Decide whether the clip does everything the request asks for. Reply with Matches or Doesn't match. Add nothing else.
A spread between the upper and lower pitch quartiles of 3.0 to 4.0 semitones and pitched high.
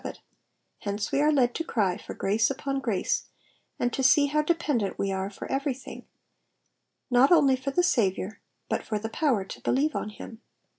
Doesn't match